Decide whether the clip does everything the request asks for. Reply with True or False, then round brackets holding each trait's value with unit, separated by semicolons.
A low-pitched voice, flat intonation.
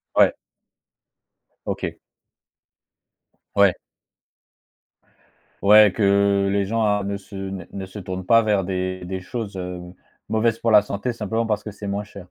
True (100 Hz; 1.8 semitones)